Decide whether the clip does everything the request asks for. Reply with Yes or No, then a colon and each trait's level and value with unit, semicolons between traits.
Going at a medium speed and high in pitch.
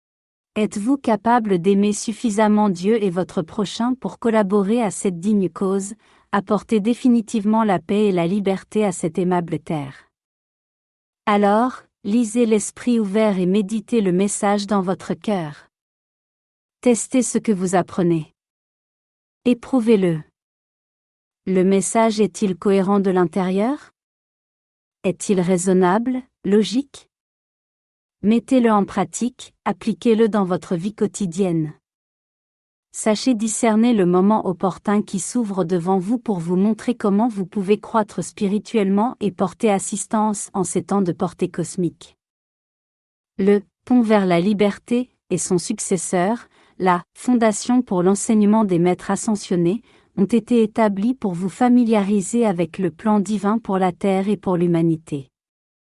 No: slow, 125 wpm; high, 205 Hz